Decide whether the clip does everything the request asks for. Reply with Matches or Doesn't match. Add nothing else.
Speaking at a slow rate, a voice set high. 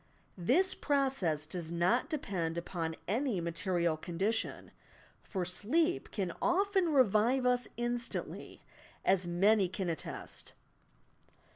Matches